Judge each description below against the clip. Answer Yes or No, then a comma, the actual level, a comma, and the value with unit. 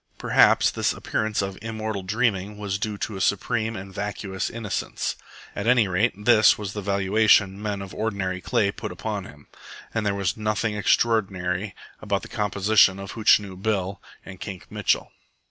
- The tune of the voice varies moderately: No, narrow, 2.1 semitones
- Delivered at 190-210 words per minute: No, average, 165 wpm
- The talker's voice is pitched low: Yes, low, 100 Hz